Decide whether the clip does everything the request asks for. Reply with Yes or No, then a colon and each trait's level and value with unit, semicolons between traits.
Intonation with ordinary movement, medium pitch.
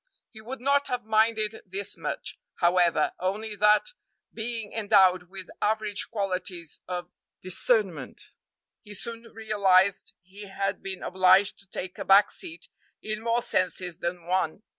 No: average, 3.0 semitones; high, 200 Hz